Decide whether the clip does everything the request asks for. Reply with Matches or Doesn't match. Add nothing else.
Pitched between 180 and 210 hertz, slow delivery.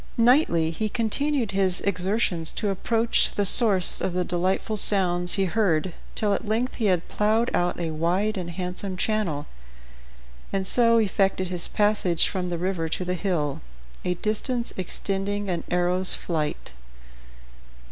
Doesn't match